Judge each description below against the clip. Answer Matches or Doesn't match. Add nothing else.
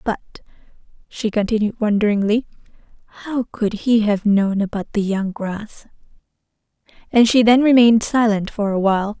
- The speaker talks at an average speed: Doesn't match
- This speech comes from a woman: Matches